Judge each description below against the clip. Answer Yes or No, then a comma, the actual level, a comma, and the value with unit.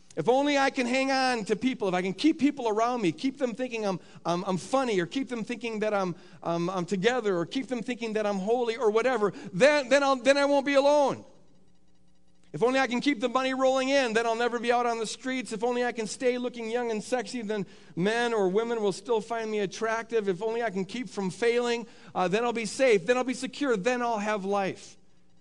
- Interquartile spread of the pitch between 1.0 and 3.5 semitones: No, average, 3.9 semitones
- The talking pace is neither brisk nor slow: No, fast, 245 wpm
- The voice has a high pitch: Yes, high, 230 Hz